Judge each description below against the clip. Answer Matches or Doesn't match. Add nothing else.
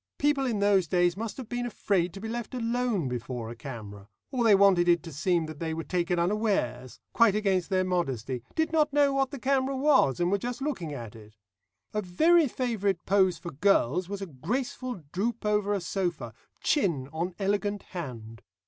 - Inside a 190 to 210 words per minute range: Matches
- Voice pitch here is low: Doesn't match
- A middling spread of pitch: Doesn't match